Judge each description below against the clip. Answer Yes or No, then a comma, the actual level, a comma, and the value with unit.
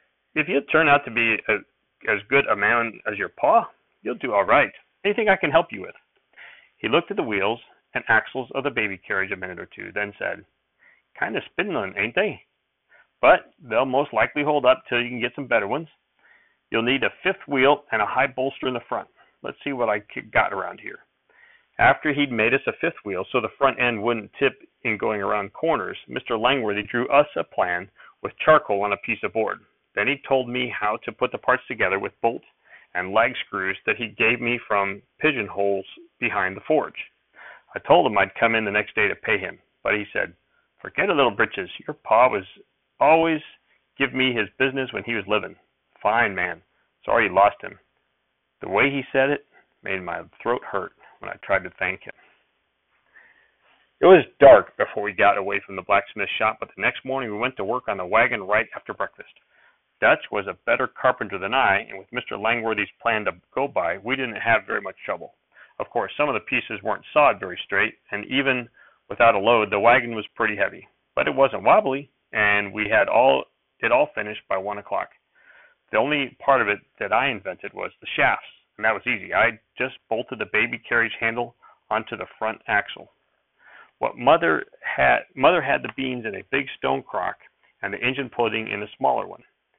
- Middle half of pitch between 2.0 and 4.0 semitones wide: No, average, 4.6 semitones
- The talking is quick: Yes, fast, 210 wpm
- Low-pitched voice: Yes, low, 120 Hz